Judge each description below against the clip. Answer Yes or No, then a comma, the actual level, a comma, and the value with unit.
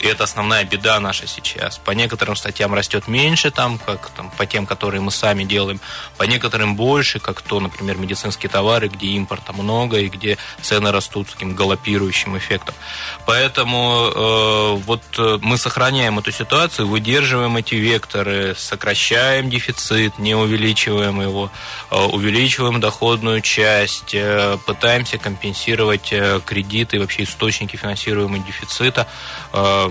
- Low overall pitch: Yes, low, 105 Hz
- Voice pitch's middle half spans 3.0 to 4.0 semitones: No, narrow, 2.5 semitones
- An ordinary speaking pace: Yes, average, 140 wpm